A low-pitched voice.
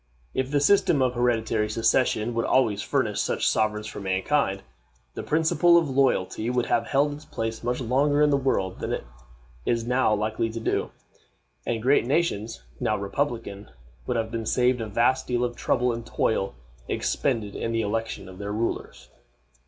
Yes: low, 115 Hz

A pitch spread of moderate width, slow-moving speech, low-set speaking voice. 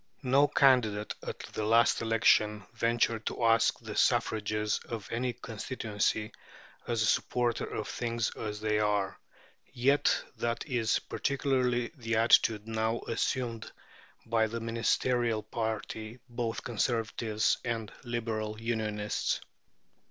No: narrow, 1.7 semitones; slow, 115 wpm; low, 115 Hz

